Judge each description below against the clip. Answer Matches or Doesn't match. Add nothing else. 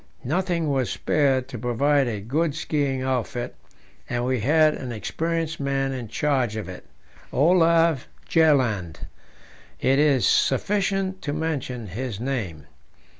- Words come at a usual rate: Doesn't match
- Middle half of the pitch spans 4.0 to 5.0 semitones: Matches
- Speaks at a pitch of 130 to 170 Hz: Matches